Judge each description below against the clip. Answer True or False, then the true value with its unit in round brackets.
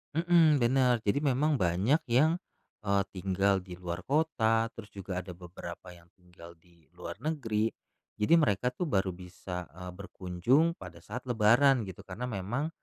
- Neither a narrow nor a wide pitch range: False (6.4 semitones)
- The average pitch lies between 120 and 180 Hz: False (105 Hz)